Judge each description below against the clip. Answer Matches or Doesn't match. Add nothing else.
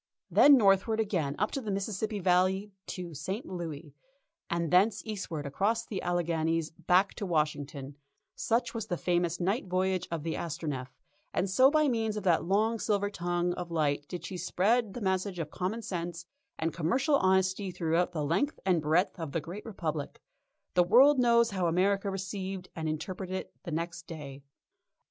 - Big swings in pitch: Doesn't match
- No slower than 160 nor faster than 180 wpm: Matches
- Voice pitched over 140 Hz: Matches